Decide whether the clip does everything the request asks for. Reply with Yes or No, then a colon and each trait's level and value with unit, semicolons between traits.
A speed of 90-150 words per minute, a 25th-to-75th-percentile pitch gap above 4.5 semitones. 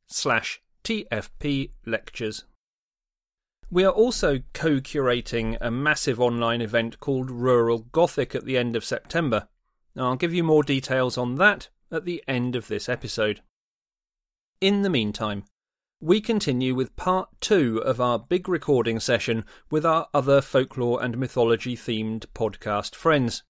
Yes: average, 140 wpm; average, 5.3 semitones